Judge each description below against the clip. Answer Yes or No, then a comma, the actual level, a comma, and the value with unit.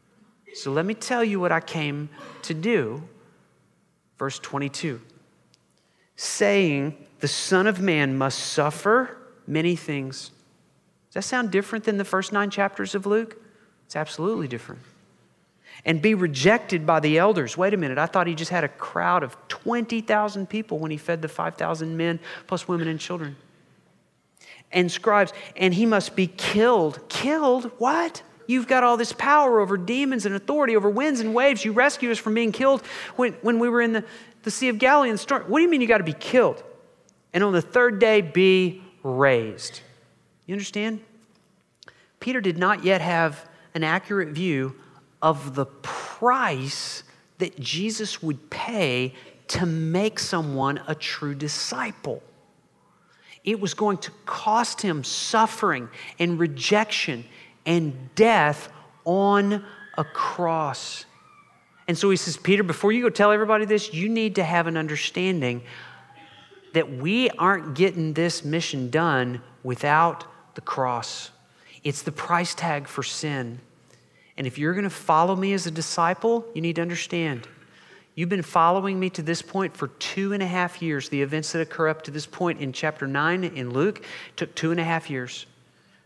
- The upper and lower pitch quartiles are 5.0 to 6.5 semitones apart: Yes, wide, 5.6 semitones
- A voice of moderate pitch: Yes, medium, 180 Hz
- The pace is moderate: Yes, average, 165 wpm